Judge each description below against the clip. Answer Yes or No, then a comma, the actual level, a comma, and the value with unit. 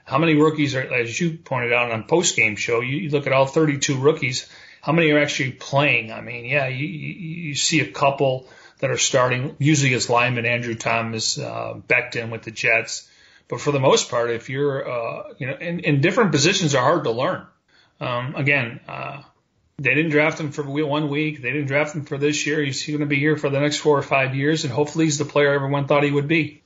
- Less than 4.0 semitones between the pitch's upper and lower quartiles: Yes, average, 2.9 semitones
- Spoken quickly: Yes, fast, 230 wpm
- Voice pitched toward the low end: No, medium, 145 Hz